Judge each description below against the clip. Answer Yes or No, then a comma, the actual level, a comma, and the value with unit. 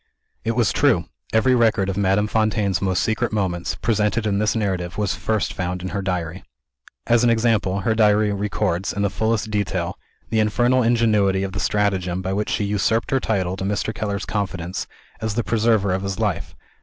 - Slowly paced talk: No, average, 190 wpm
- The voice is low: Yes, low, 105 Hz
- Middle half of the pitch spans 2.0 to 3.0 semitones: Yes, average, 2.7 semitones